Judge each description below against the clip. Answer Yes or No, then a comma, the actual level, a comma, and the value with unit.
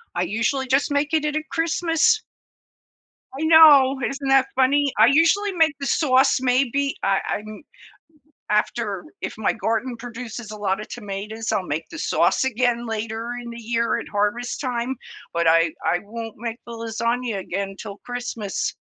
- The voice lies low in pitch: No, high, 235 Hz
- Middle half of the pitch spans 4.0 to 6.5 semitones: Yes, average, 4.3 semitones